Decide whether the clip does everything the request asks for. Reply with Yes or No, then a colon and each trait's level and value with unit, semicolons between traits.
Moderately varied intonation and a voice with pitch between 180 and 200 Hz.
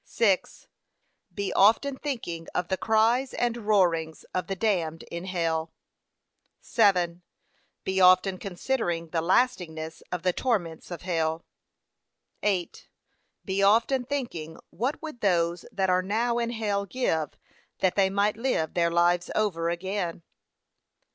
Yes: average, 4.5 semitones; high, 190 Hz